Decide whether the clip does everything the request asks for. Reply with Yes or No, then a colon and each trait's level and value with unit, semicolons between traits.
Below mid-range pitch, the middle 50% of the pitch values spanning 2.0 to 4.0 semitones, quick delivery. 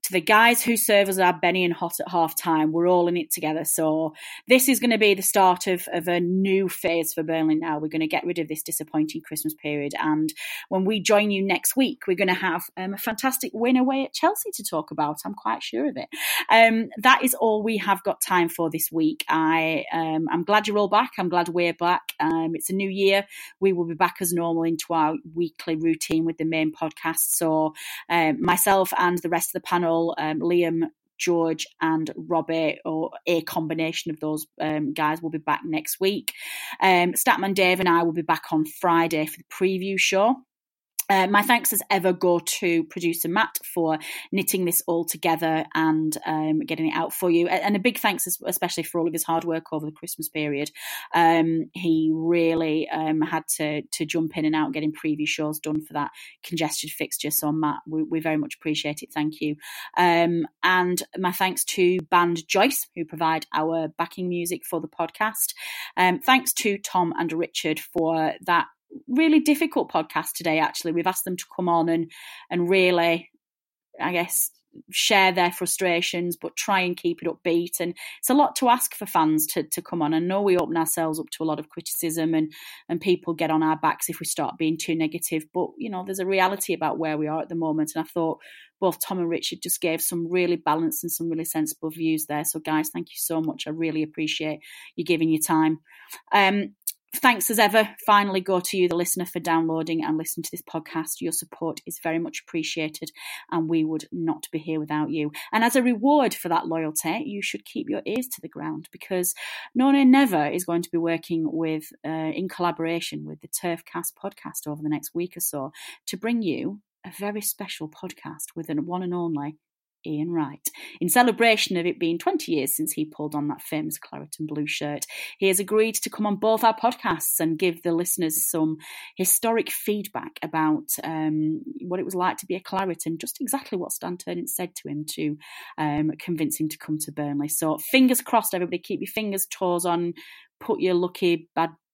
No: medium, 170 Hz; average, 3.3 semitones; fast, 210 wpm